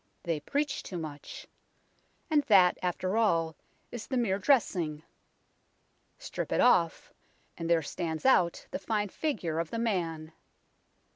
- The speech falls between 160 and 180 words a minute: No, slow, 135 wpm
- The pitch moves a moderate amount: No, wide, 5.7 semitones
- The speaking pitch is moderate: Yes, medium, 180 Hz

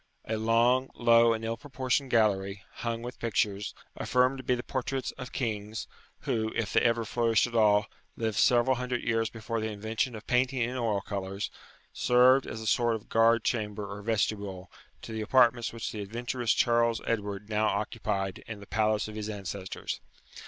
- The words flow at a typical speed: Yes, average, 180 wpm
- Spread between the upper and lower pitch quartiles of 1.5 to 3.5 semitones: Yes, narrow, 2.4 semitones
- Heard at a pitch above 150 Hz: No, low, 115 Hz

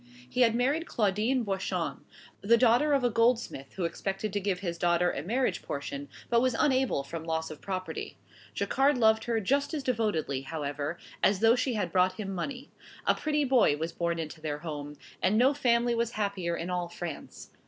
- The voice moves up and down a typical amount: No, wide, 6.4 semitones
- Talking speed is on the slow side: No, average, 190 wpm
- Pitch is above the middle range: Yes, high, 200 Hz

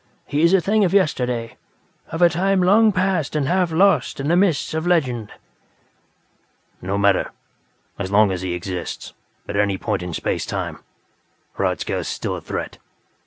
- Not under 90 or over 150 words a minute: No, average, 165 wpm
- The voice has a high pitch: No, medium, 150 Hz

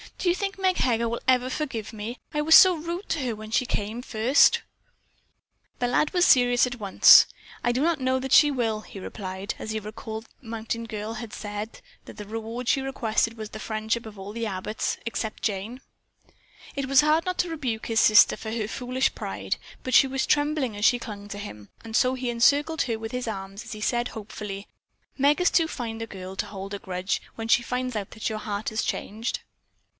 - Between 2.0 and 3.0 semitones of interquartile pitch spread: No, average, 3.4 semitones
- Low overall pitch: No, high, 230 Hz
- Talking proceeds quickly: Yes, fast, 215 wpm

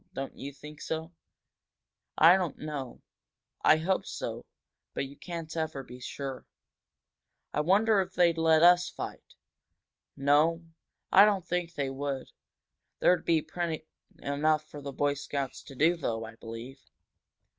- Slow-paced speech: No, average, 145 wpm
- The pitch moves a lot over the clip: No, average, 3.5 semitones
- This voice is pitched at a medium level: Yes, medium, 155 Hz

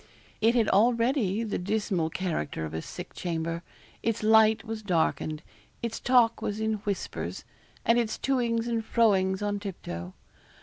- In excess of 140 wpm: Yes, average, 165 wpm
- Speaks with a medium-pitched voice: No, high, 215 Hz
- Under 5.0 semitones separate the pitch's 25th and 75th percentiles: Yes, average, 4.0 semitones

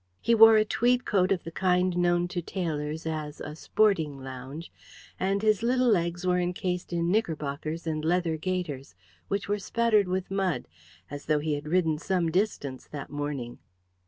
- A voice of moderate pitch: Yes, medium, 175 Hz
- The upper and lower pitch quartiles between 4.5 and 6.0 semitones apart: No, average, 4.1 semitones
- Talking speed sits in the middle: Yes, average, 170 wpm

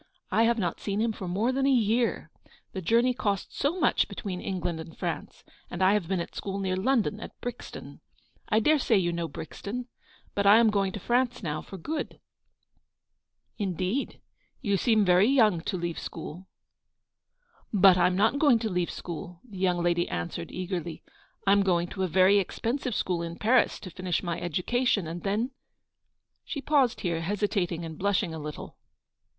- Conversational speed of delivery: Yes, average, 190 wpm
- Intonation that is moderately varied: Yes, average, 4.6 semitones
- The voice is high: Yes, high, 195 Hz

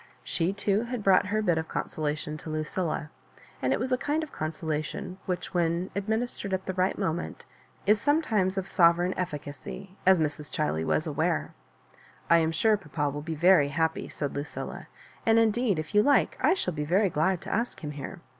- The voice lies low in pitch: No, medium, 180 Hz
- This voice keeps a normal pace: Yes, average, 190 wpm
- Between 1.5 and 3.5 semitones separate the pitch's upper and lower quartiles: No, average, 4.6 semitones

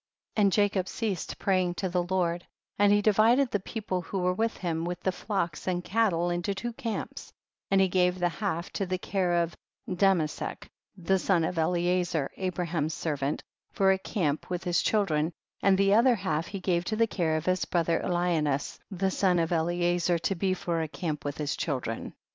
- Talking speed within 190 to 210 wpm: Yes, average, 195 wpm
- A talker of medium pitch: Yes, medium, 180 Hz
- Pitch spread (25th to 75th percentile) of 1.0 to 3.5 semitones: Yes, narrow, 2.6 semitones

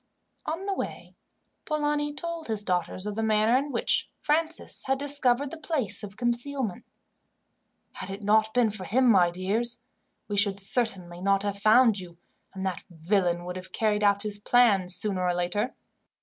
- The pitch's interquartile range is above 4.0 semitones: Yes, average, 4.8 semitones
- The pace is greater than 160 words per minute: Yes, average, 170 wpm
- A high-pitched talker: Yes, high, 210 Hz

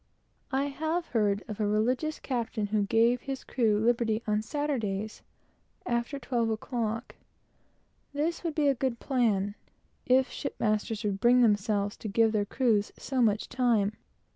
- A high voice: Yes, high, 230 Hz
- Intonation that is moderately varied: Yes, average, 3.6 semitones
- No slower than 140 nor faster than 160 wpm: Yes, average, 145 wpm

